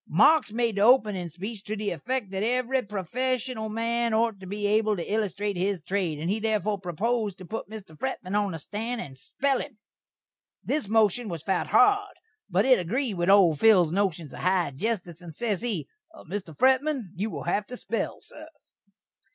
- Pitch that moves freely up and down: No, average, 4.1 semitones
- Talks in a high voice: Yes, high, 210 Hz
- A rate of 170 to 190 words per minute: Yes, average, 185 wpm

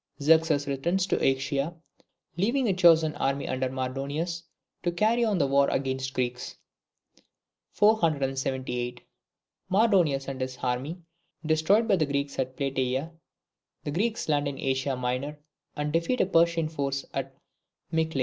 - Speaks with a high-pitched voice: No, medium, 145 Hz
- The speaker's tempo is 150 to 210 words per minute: No, average, 140 wpm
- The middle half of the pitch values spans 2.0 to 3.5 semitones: No, average, 4.2 semitones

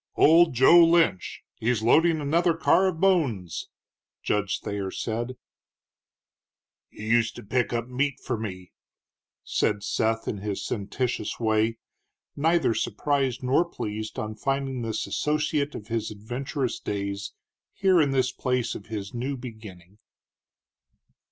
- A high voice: No, low, 120 Hz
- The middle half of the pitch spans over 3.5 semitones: Yes, average, 4.9 semitones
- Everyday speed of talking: No, slow, 130 wpm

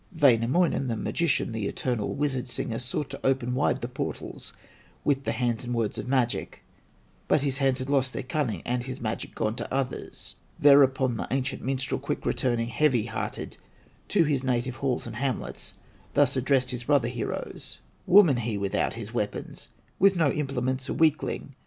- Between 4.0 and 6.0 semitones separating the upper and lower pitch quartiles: No, narrow, 2.5 semitones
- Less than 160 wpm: No, average, 170 wpm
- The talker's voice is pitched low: Yes, low, 130 Hz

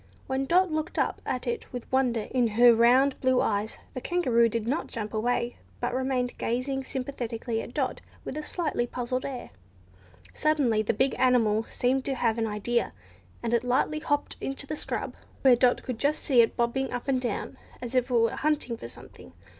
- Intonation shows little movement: Yes, narrow, 2.3 semitones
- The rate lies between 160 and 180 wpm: No, average, 195 wpm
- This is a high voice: Yes, very high, 250 Hz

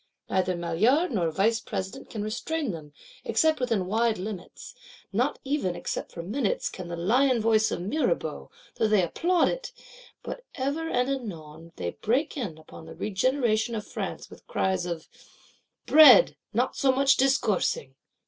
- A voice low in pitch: No, high, 220 Hz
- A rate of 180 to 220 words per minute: No, average, 155 wpm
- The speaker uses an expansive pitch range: Yes, wide, 6.9 semitones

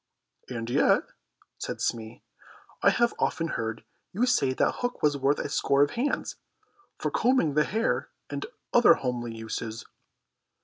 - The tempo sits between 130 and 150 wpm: Yes, average, 145 wpm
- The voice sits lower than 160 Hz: Yes, medium, 140 Hz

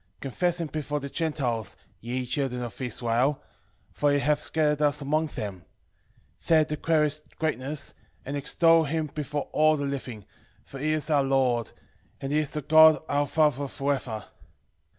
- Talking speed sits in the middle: Yes, average, 170 wpm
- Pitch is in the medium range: Yes, medium, 145 Hz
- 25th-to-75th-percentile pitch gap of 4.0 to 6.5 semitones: No, average, 2.7 semitones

